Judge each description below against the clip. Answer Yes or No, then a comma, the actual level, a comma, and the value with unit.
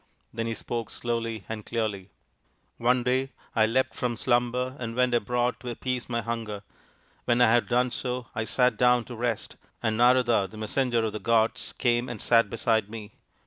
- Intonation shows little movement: Yes, narrow, 1.8 semitones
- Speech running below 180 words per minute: No, average, 185 wpm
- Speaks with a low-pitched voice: Yes, low, 120 Hz